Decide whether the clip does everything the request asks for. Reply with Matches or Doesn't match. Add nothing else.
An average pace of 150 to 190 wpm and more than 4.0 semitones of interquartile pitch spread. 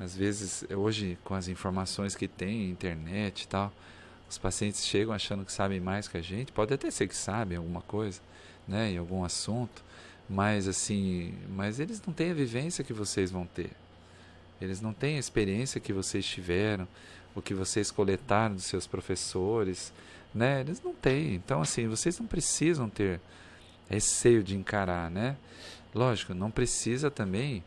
Doesn't match